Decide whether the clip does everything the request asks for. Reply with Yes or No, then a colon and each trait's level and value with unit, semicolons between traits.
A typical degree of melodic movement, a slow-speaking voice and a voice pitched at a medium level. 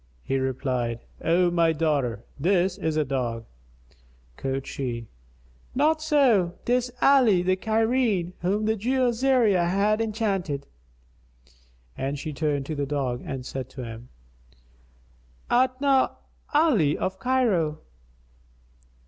No: wide, 8.7 semitones; slow, 120 wpm; medium, 175 Hz